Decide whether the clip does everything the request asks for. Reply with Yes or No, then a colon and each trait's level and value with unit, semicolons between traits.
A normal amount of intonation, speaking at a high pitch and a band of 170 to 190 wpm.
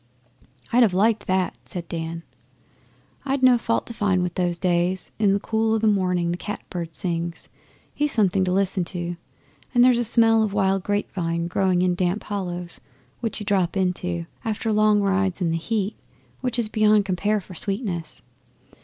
Yes: average, 3.4 semitones; high, 195 Hz; average, 180 wpm